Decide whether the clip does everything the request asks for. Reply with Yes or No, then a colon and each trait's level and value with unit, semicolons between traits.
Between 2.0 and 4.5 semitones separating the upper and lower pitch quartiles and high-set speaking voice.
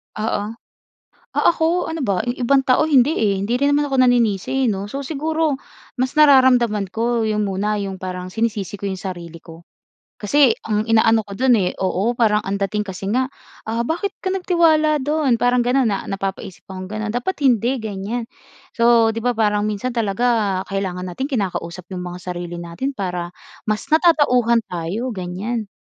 No: average, 4.9 semitones; high, 220 Hz